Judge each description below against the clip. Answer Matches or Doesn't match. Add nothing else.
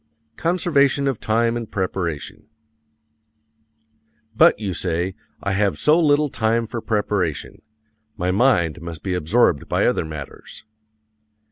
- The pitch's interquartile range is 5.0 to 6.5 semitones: Matches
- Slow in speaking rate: Matches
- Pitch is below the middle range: Matches